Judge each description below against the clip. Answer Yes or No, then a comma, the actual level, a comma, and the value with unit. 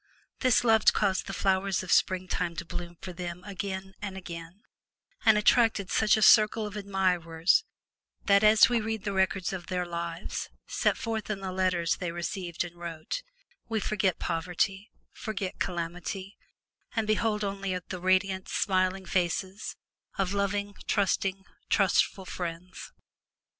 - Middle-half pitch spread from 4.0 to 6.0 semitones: No, narrow, 2.5 semitones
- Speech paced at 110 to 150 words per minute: Yes, average, 140 wpm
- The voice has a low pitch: No, high, 190 Hz